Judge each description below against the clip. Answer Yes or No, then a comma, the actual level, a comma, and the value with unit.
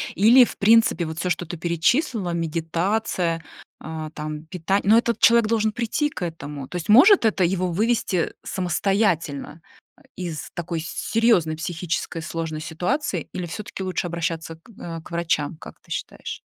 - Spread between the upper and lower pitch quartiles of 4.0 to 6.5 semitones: Yes, average, 4.6 semitones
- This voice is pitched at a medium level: Yes, medium, 175 Hz